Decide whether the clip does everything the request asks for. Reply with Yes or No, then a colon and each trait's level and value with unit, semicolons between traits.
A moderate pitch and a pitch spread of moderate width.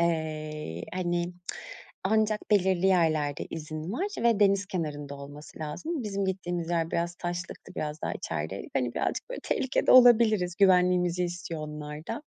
Yes: medium, 175 Hz; average, 4.0 semitones